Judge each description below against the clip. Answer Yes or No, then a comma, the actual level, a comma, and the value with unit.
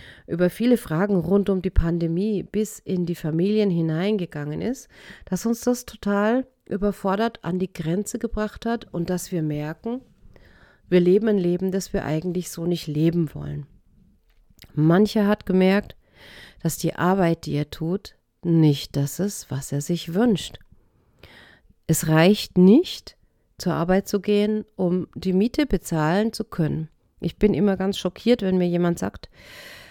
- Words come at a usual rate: Yes, average, 155 wpm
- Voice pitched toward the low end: No, medium, 185 Hz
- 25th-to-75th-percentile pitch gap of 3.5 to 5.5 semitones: Yes, average, 4.0 semitones